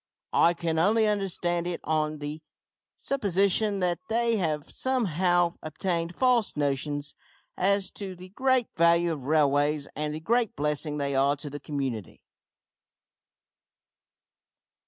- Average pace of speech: No, slow, 125 wpm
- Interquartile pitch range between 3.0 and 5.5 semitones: Yes, average, 5.0 semitones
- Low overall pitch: No, medium, 170 Hz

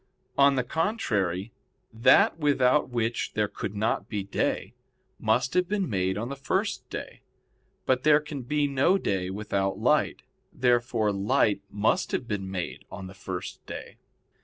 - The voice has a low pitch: Yes, low, 115 Hz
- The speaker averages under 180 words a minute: Yes, average, 155 wpm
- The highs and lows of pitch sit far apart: Yes, wide, 5.8 semitones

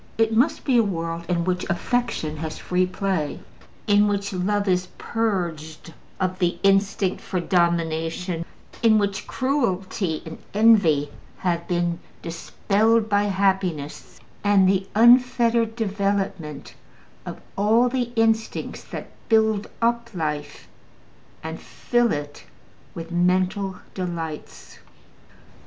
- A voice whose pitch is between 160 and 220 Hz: Yes, high, 190 Hz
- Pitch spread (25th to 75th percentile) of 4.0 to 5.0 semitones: Yes, average, 4.3 semitones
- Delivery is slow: Yes, slow, 115 wpm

